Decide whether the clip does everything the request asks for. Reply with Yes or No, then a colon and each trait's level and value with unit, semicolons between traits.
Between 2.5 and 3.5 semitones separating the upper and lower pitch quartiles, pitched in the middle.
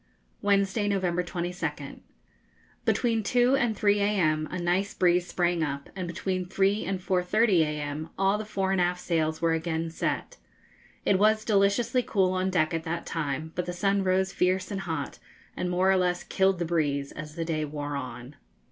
Yes: average, 3.2 semitones; medium, 180 Hz